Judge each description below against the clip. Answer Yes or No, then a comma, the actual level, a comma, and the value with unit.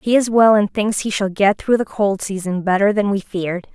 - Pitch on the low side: No, high, 200 Hz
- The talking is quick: Yes, fast, 255 wpm